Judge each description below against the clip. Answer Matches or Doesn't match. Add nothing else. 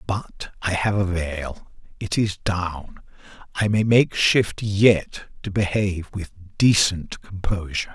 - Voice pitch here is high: Doesn't match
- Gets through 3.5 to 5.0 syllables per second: Matches